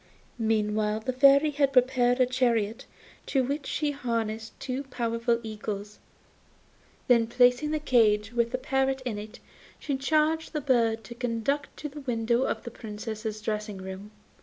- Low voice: No, high, 240 Hz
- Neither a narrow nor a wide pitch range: Yes, average, 3.5 semitones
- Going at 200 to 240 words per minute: No, average, 160 wpm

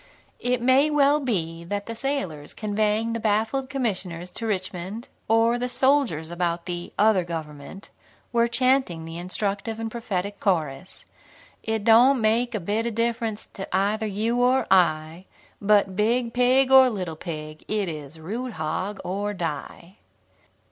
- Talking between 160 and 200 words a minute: No, average, 150 wpm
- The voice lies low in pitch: No, high, 210 Hz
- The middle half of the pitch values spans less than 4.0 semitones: No, average, 5.1 semitones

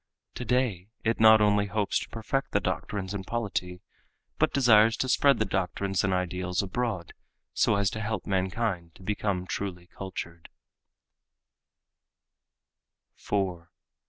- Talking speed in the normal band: No, slow, 125 wpm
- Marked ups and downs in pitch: No, average, 3.2 semitones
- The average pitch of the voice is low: Yes, low, 100 Hz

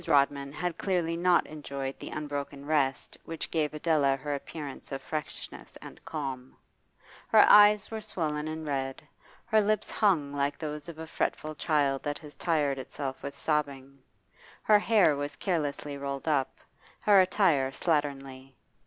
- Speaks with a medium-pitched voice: Yes, medium, 150 Hz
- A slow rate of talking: No, average, 150 wpm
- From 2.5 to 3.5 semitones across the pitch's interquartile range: Yes, average, 2.9 semitones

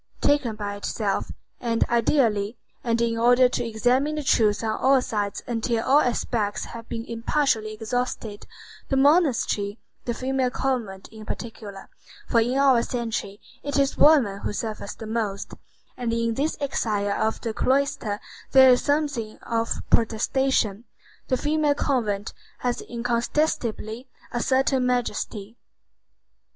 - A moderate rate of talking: No, slow, 130 wpm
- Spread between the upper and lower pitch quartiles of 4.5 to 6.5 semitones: No, average, 3.4 semitones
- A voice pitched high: Yes, high, 235 Hz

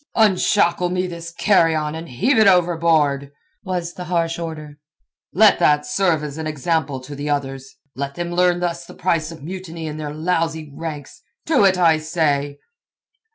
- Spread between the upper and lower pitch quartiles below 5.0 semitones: Yes, average, 2.9 semitones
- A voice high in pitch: No, medium, 165 Hz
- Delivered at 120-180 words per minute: Yes, average, 165 wpm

